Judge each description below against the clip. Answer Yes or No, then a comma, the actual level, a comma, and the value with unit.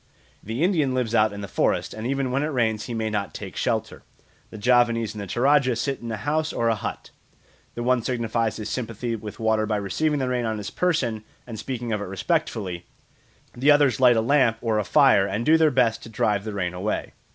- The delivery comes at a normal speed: No, fast, 225 wpm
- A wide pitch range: No, average, 3.3 semitones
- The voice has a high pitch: No, low, 115 Hz